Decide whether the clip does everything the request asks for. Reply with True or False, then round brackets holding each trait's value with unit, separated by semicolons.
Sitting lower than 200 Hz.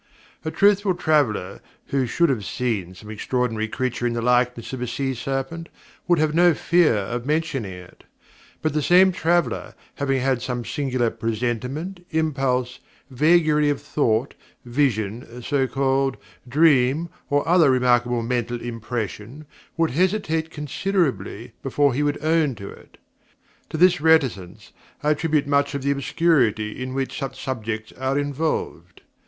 True (135 Hz)